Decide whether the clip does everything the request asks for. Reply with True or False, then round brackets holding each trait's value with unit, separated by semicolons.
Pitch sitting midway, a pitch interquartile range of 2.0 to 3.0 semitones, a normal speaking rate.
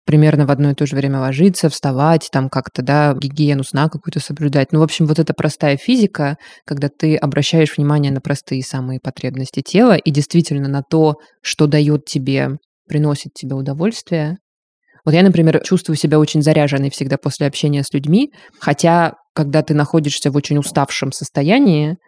False (150 Hz; 2.4 semitones; 170 wpm)